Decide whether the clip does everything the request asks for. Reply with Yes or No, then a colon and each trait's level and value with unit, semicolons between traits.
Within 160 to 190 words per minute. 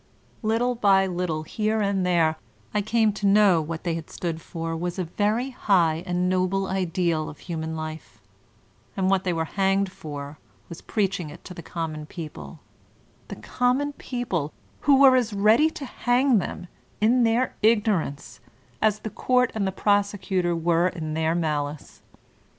Yes: average, 165 wpm